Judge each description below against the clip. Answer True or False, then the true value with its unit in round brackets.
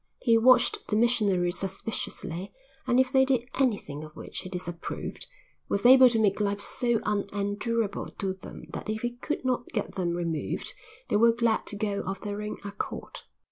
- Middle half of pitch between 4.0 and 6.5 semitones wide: False (3.6 semitones)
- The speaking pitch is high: True (210 Hz)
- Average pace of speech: True (180 wpm)